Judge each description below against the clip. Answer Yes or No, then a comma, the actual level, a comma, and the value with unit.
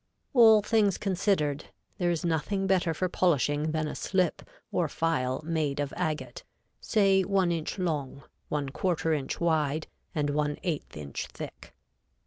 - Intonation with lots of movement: No, average, 4.0 semitones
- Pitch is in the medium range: Yes, medium, 160 Hz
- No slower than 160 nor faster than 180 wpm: No, average, 145 wpm